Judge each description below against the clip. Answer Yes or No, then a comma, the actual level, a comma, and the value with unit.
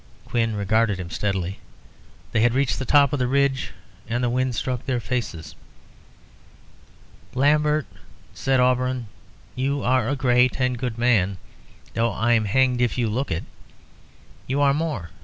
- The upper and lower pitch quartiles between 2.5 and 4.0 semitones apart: Yes, average, 2.8 semitones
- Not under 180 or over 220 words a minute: No, average, 150 wpm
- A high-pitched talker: No, low, 125 Hz